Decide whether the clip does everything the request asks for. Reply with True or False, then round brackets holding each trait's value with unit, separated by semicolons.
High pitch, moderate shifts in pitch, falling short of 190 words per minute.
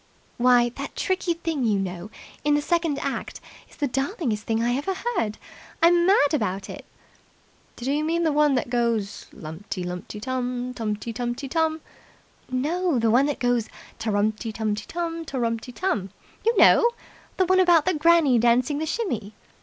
False (255 Hz; 6.4 semitones; 170 wpm)